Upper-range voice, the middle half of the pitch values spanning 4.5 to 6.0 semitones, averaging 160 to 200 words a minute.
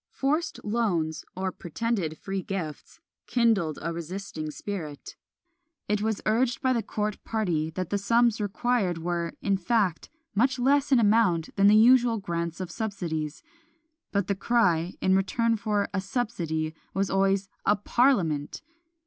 No: high, 200 Hz; average, 5.1 semitones; average, 145 wpm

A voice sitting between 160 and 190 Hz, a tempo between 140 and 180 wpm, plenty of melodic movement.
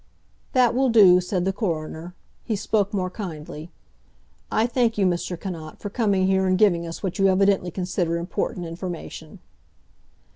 No: medium, 185 Hz; average, 155 wpm; average, 2.9 semitones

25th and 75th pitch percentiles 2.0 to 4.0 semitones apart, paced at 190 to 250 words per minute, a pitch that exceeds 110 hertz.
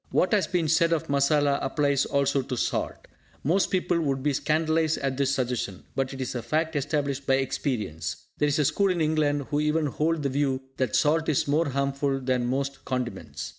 Yes: average, 2.7 semitones; average, 200 wpm; medium, 140 Hz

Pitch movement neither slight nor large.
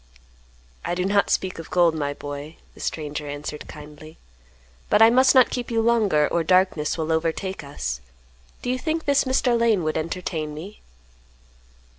No: wide, 6.8 semitones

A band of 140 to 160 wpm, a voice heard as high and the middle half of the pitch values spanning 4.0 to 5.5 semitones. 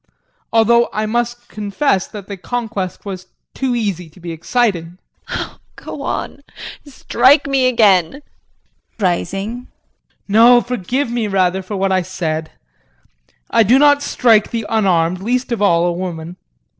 Yes: average, 145 wpm; high, 210 Hz; average, 4.7 semitones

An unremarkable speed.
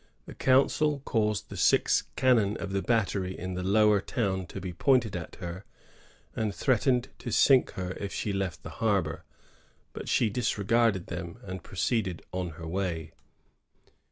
Yes: average, 155 wpm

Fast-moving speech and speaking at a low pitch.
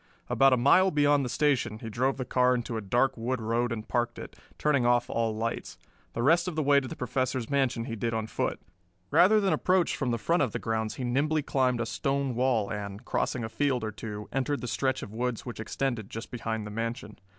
Yes: fast, 230 wpm; low, 125 Hz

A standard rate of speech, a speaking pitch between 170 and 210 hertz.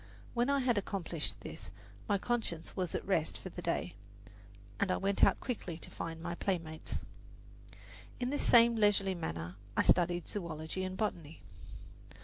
Yes: average, 155 wpm; medium, 185 Hz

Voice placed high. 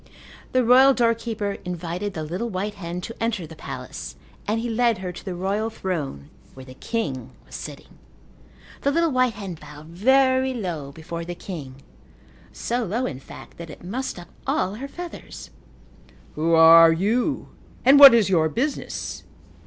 Yes: high, 195 Hz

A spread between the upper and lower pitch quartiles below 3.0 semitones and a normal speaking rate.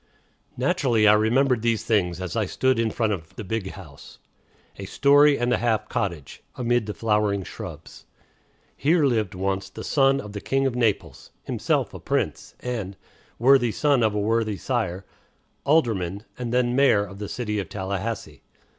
No: average, 3.8 semitones; average, 170 wpm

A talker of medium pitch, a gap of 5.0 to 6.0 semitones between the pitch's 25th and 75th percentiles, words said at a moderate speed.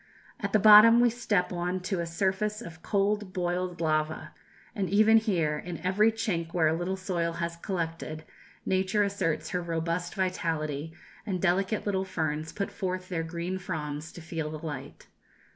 No: medium, 180 Hz; average, 3.1 semitones; average, 165 wpm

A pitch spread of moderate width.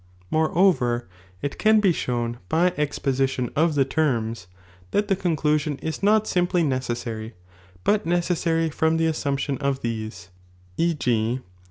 No: wide, 5.7 semitones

